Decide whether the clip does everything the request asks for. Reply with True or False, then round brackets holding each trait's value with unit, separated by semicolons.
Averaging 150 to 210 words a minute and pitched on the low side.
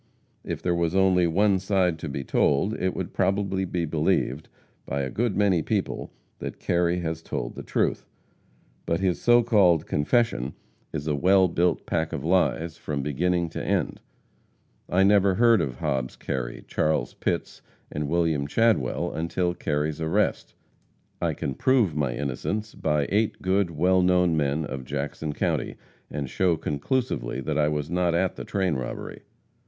True (160 wpm; 85 Hz)